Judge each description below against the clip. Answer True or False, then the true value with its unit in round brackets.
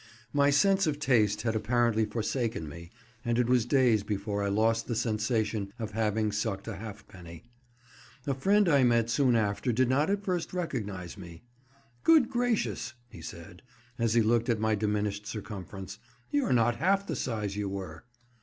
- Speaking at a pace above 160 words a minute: True (170 wpm)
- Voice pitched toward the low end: True (110 Hz)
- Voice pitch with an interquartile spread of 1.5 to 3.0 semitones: False (3.9 semitones)